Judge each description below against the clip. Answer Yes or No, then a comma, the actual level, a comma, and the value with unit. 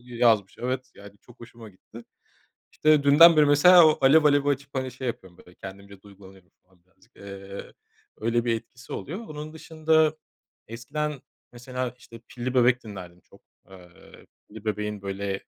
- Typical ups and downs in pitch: No, wide, 6.2 semitones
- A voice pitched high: No, low, 120 Hz